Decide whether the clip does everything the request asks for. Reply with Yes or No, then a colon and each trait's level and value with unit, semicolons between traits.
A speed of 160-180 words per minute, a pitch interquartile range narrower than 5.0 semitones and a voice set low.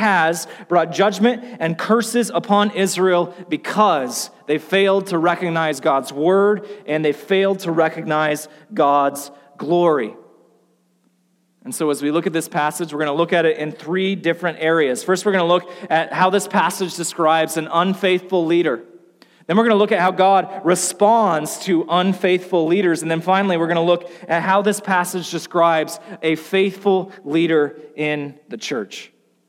No: average, 165 wpm; average, 3.2 semitones; medium, 175 Hz